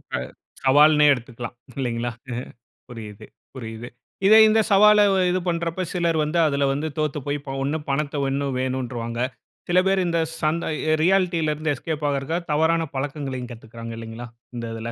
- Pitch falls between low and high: Yes, medium, 145 Hz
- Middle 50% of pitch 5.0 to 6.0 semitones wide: Yes, average, 5.3 semitones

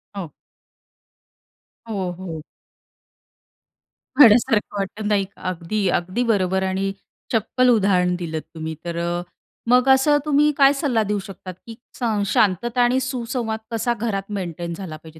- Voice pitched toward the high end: Yes, high, 205 Hz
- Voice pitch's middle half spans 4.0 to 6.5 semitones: Yes, average, 4.7 semitones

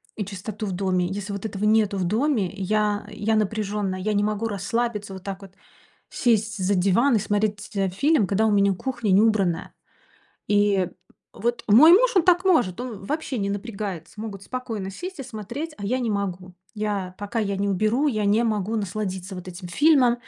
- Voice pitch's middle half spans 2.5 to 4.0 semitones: Yes, average, 2.8 semitones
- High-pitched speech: Yes, high, 210 Hz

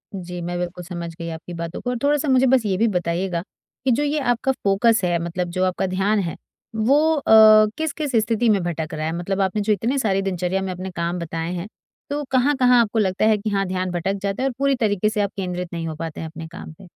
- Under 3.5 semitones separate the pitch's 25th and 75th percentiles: No, average, 4.6 semitones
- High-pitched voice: Yes, high, 195 Hz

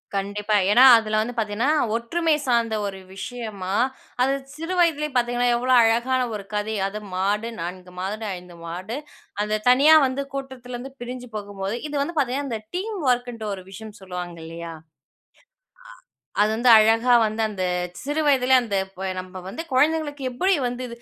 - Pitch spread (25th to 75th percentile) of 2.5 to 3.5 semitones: No, average, 4.2 semitones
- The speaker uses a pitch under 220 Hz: No, high, 235 Hz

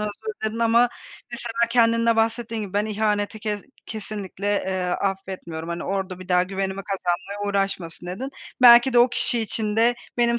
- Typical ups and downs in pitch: Yes, average, 3.2 semitones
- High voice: Yes, high, 210 Hz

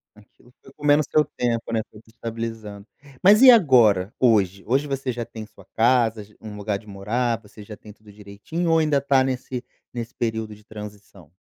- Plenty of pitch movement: No, average, 3.6 semitones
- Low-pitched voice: Yes, low, 115 Hz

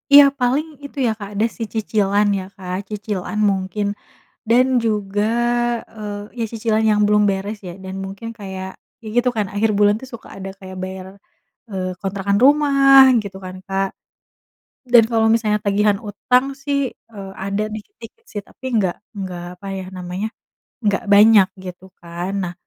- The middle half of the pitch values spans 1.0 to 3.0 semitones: Yes, narrow, 2.6 semitones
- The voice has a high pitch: Yes, high, 205 Hz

